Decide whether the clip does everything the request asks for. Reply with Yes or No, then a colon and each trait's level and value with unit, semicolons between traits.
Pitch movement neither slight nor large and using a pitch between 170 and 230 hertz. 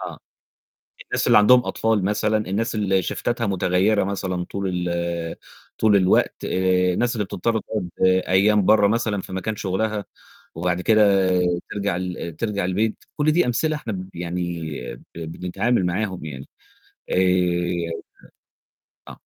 No: average, 3.2 semitones; very low, 95 Hz